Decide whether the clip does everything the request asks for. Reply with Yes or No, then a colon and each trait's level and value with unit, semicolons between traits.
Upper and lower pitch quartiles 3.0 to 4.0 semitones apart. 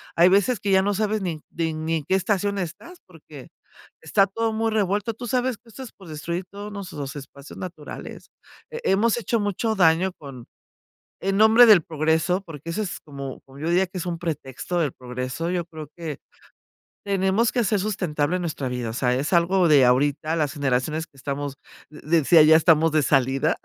No: average, 5.2 semitones